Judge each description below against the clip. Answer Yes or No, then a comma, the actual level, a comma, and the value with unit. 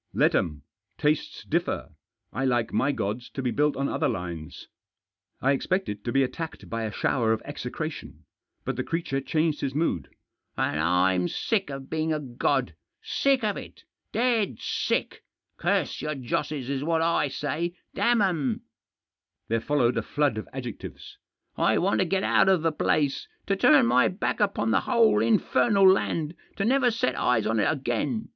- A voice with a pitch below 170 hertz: Yes, medium, 140 Hz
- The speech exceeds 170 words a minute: Yes, average, 185 wpm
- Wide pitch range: Yes, wide, 6.7 semitones